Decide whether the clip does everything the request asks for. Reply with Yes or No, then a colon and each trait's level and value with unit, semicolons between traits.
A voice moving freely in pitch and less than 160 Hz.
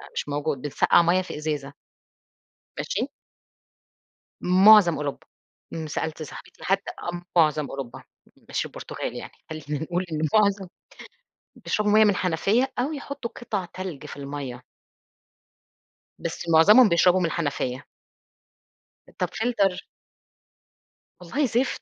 No: wide, 5.8 semitones; medium, 175 Hz